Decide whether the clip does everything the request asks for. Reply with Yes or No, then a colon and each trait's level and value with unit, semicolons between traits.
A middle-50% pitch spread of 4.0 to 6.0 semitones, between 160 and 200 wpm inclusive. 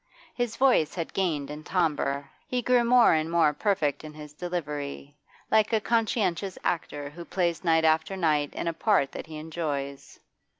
Yes: average, 4.5 semitones; average, 170 wpm